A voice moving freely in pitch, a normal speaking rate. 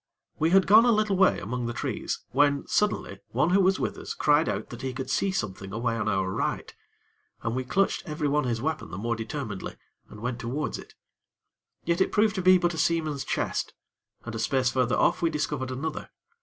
No: wide, 6.7 semitones; fast, 210 wpm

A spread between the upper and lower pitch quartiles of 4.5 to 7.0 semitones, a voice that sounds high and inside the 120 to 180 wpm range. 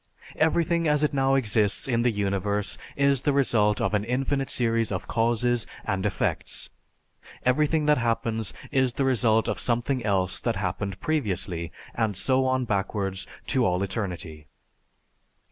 No: average, 4.8 semitones; low, 115 Hz; average, 145 wpm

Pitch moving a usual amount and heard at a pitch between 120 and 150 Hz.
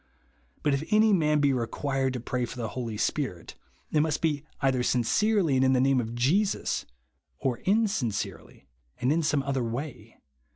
Yes: average, 3.8 semitones; low, 135 Hz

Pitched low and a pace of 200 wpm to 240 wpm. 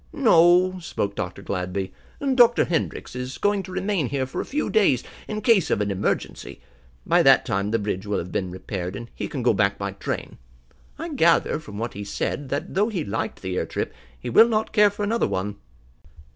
Yes: low, 130 Hz; fast, 205 wpm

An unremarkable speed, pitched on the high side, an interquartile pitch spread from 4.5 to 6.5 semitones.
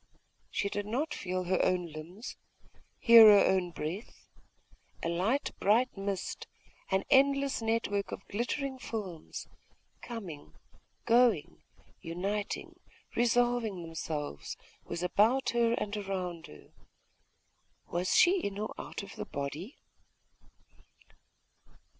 No: slow, 115 wpm; high, 200 Hz; average, 4.8 semitones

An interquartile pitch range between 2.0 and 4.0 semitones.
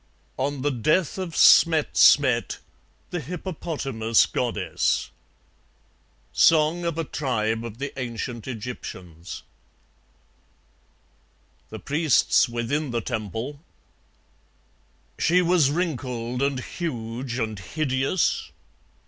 No: average, 5.0 semitones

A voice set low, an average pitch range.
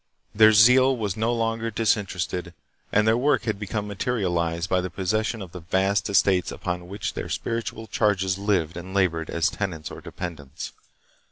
Yes: low, 100 Hz; average, 3.8 semitones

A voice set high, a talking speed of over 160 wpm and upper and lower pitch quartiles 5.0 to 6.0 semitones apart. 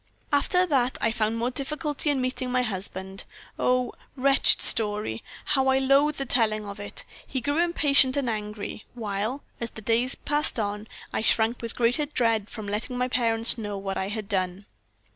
No: high, 235 Hz; average, 180 wpm; average, 4.1 semitones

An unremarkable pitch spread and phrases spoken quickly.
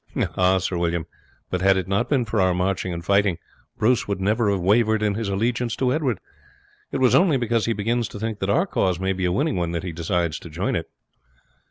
Yes: average, 4.2 semitones; fast, 230 wpm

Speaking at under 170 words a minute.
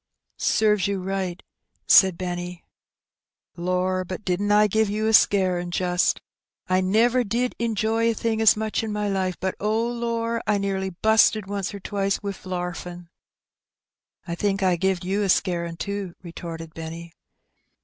Yes: average, 160 wpm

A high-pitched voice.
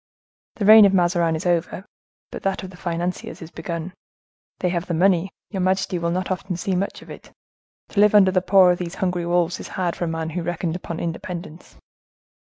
No: medium, 180 Hz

